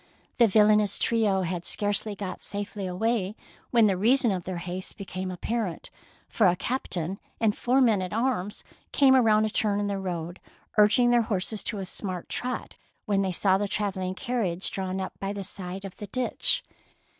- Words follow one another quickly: No, average, 185 wpm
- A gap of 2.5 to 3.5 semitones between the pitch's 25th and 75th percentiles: Yes, average, 2.9 semitones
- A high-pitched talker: Yes, high, 200 Hz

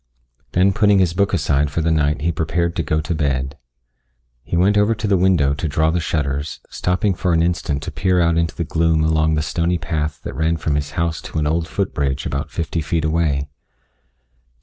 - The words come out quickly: Yes, fast, 215 wpm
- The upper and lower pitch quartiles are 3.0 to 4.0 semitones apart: No, narrow, 2.5 semitones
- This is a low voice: Yes, very low, 80 Hz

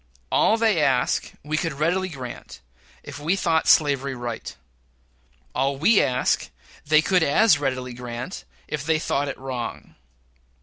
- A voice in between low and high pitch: Yes, medium, 145 Hz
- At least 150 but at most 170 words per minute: No, average, 140 wpm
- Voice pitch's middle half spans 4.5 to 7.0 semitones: No, average, 4.0 semitones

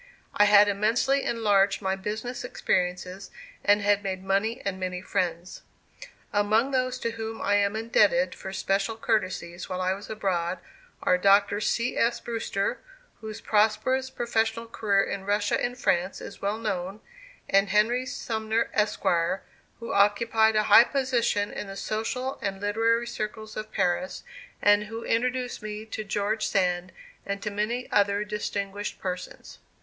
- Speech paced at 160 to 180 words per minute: No, average, 150 wpm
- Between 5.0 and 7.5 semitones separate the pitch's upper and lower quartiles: No, narrow, 2.4 semitones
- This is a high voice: Yes, high, 210 Hz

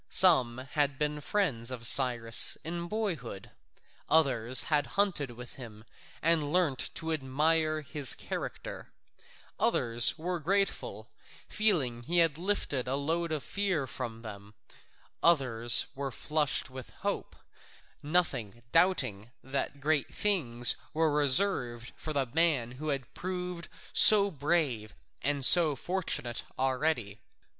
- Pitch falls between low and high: Yes, medium, 145 Hz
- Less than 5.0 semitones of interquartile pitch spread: No, wide, 5.5 semitones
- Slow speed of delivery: Yes, slow, 120 wpm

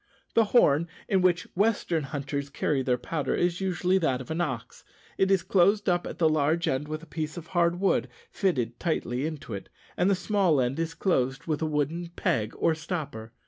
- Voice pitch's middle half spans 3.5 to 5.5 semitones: Yes, average, 4.2 semitones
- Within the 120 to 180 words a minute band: No, average, 200 wpm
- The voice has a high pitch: No, medium, 160 Hz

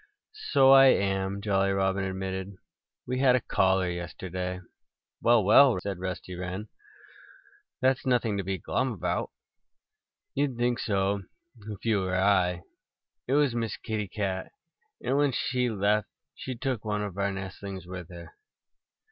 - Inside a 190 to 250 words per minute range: No, average, 145 wpm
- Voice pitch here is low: Yes, low, 100 Hz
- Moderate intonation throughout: Yes, average, 4.2 semitones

